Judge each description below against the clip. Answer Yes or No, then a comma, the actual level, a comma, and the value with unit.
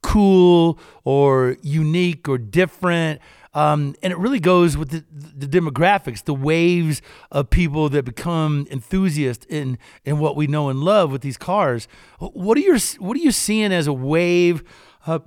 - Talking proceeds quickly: No, average, 170 wpm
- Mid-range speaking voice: Yes, medium, 160 Hz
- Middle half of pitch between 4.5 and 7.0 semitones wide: No, average, 3.9 semitones